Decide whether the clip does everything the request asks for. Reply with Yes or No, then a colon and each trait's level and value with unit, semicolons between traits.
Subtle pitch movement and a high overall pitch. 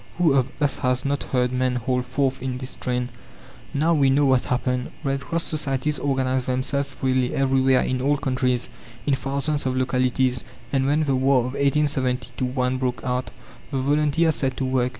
No: narrow, 1.7 semitones; low, 130 Hz